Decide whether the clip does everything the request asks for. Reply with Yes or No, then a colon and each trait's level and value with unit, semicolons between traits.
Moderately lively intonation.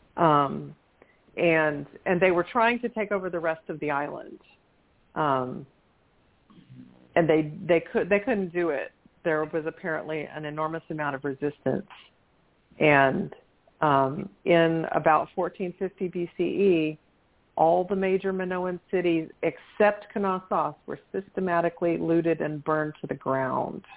Yes: average, 3.4 semitones